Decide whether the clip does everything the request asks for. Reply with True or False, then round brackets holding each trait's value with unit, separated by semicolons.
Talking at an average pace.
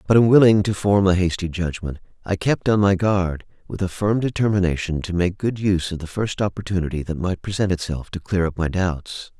False (210 wpm)